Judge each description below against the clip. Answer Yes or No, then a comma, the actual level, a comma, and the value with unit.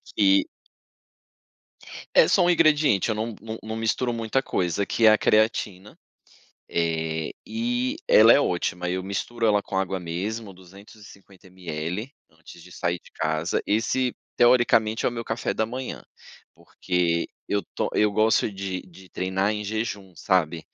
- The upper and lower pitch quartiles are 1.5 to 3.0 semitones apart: No, average, 3.9 semitones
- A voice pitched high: No, low, 100 Hz